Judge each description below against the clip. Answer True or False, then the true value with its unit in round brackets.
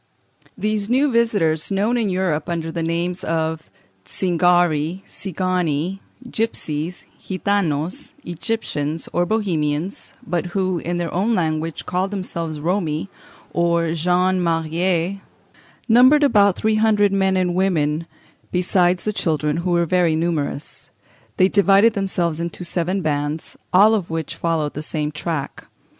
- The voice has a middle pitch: True (175 Hz)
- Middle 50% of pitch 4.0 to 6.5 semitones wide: False (3.3 semitones)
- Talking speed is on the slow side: True (130 wpm)